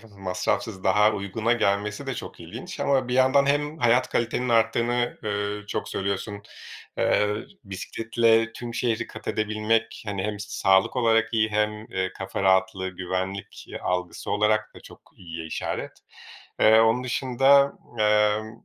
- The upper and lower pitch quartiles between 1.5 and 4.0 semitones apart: Yes, average, 2.8 semitones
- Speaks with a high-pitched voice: No, low, 105 Hz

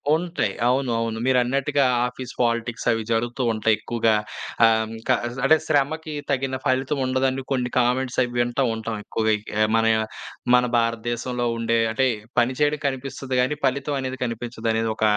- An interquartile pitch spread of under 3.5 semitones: Yes, narrow, 2.6 semitones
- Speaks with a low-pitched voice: Yes, low, 125 Hz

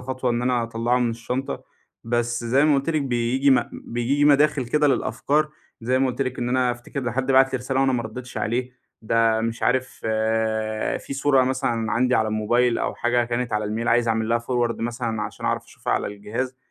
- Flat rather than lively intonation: Yes, narrow, 2.1 semitones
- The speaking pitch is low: Yes, low, 120 Hz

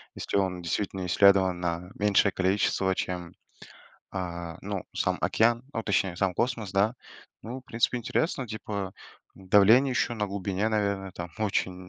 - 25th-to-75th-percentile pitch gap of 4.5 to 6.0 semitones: No, average, 2.9 semitones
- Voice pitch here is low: Yes, low, 100 Hz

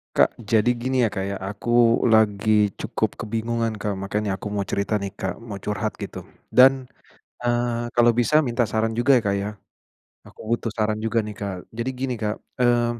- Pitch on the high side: No, low, 110 Hz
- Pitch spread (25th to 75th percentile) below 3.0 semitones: Yes, narrow, 2.5 semitones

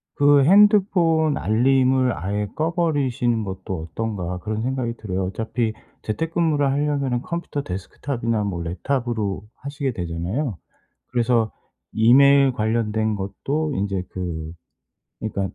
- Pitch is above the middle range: No, low, 120 Hz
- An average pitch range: No, wide, 5.7 semitones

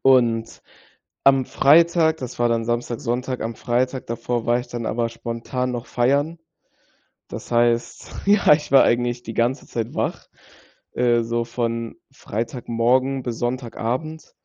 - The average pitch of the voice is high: No, low, 120 Hz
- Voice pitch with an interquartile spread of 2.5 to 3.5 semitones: No, narrow, 1.9 semitones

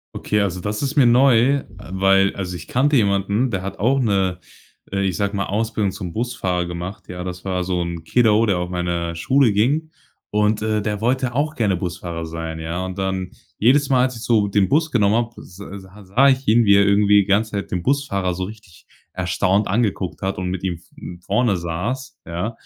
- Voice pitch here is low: Yes, low, 100 Hz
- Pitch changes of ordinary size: Yes, average, 4.1 semitones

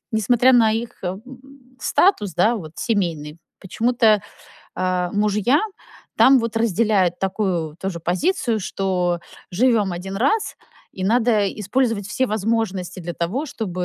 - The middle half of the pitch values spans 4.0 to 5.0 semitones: Yes, average, 4.5 semitones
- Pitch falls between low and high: No, high, 210 Hz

